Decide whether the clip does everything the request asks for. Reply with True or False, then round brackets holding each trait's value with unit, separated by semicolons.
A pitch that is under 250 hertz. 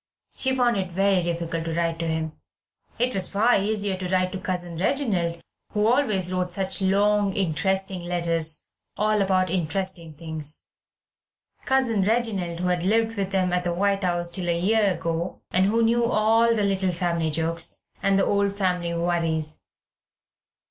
True (185 Hz)